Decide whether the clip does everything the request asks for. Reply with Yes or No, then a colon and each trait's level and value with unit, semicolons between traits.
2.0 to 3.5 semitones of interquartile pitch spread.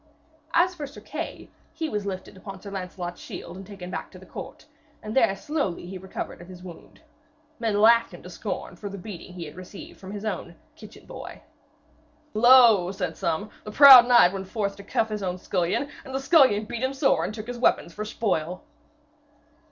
No: average, 4.5 semitones